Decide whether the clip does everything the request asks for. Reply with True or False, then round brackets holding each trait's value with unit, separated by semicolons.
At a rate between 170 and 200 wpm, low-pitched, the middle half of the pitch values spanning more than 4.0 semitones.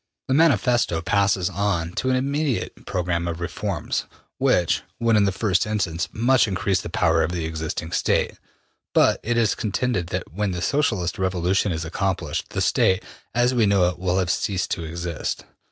True (180 wpm; 95 Hz; 4.5 semitones)